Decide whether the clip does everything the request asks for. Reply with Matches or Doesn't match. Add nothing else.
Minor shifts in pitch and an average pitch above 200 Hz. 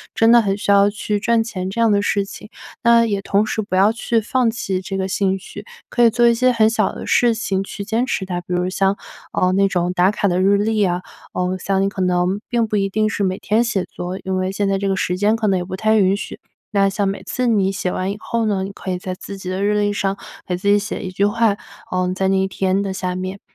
Doesn't match